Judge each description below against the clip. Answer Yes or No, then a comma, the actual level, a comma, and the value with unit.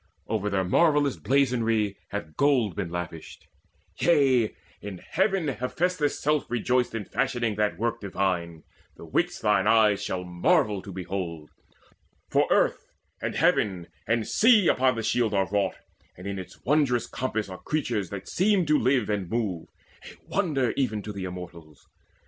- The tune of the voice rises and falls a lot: Yes, wide, 6.1 semitones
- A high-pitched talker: No, low, 110 Hz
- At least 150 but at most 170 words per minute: Yes, average, 155 wpm